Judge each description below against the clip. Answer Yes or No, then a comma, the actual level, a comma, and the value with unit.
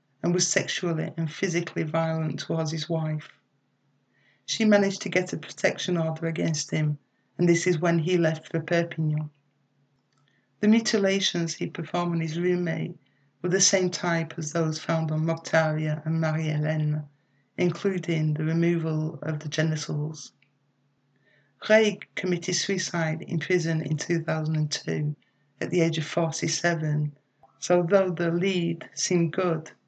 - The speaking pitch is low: No, medium, 160 Hz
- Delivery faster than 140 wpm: No, slow, 135 wpm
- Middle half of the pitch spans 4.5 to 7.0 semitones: No, narrow, 2.5 semitones